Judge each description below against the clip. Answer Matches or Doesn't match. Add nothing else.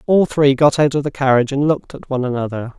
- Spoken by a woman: Doesn't match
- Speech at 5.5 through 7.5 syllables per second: Matches